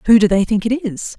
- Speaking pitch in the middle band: No, high, 215 Hz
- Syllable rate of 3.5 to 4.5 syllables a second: No, 5.9 syllables/s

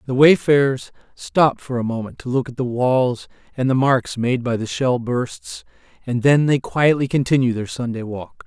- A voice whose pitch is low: Yes, low, 125 Hz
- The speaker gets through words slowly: No, average, 190 wpm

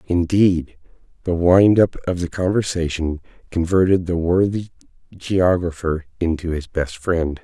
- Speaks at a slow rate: Yes, slow, 120 wpm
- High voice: No, very low, 85 Hz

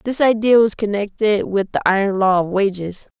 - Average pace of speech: Yes, average, 190 wpm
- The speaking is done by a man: No, female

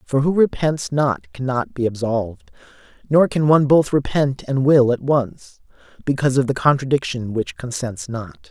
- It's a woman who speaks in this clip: No, male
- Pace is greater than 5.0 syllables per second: No, 4.7 syllables/s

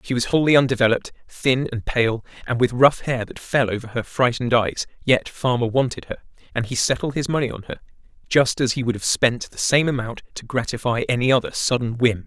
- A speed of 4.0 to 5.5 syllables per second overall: No, 5.7 syllables/s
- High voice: No, low, 125 Hz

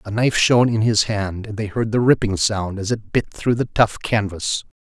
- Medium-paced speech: No, fast, 235 wpm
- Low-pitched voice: Yes, low, 105 Hz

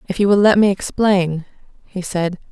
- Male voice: No, female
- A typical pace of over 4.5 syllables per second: Yes, 4.8 syllables/s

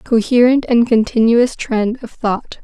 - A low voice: No, high, 235 Hz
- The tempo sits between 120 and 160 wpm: Yes, slow, 135 wpm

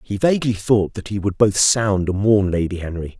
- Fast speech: Yes, fast, 225 wpm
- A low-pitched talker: Yes, low, 100 Hz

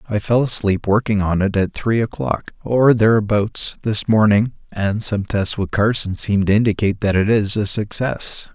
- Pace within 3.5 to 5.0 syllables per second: Yes, 4.6 syllables/s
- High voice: No, low, 105 Hz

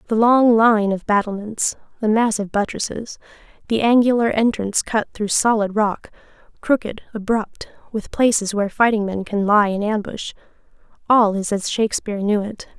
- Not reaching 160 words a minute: Yes, average, 150 wpm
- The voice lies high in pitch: Yes, high, 215 Hz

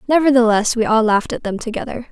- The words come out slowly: No, average, 200 wpm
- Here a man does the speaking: No, female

